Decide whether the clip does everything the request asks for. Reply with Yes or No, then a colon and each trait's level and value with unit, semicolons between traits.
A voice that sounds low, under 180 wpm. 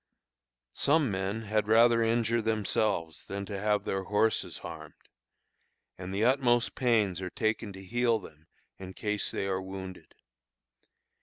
Yes: low, 105 Hz; slow, 135 wpm